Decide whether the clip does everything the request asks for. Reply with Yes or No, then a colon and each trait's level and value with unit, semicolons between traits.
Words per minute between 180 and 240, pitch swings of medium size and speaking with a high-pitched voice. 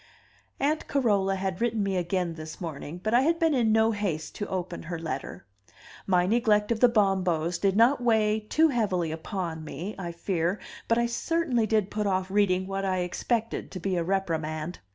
Yes: average, 190 wpm; average, 4.1 semitones; high, 195 Hz